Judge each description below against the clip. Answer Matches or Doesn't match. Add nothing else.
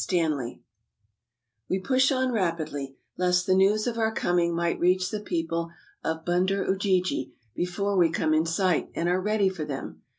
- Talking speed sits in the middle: Matches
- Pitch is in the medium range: Matches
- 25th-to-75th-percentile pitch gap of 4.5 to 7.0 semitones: Doesn't match